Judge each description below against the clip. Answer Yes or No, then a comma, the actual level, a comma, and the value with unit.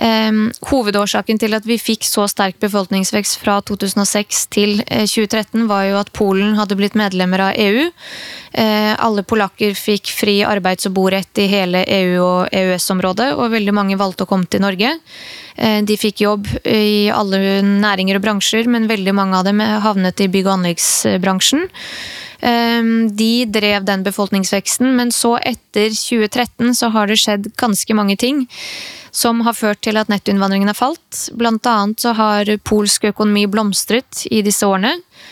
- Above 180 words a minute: No, average, 160 wpm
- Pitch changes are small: Yes, narrow, 2.0 semitones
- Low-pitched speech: No, high, 210 Hz